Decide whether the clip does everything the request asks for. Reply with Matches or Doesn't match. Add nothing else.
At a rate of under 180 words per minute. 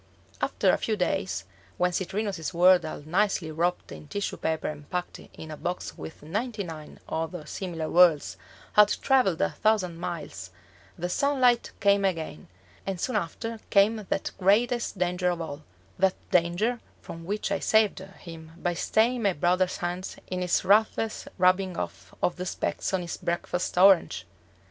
Matches